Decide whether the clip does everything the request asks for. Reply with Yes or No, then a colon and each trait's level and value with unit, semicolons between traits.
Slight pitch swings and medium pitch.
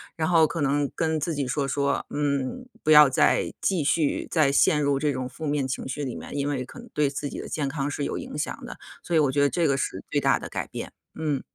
Yes: narrow, 2.1 semitones; medium, 145 Hz